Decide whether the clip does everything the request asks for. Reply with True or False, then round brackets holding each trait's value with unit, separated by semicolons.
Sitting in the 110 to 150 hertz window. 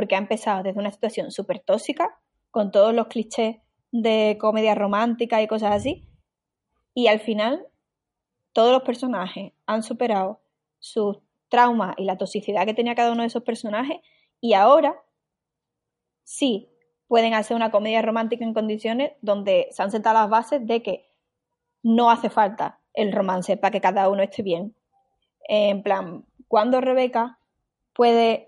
False (225 Hz)